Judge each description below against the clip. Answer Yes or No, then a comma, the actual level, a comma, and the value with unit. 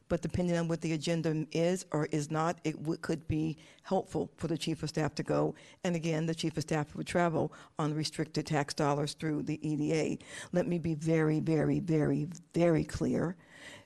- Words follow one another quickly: No, average, 195 wpm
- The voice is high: No, medium, 160 Hz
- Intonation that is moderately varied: No, narrow, 1.7 semitones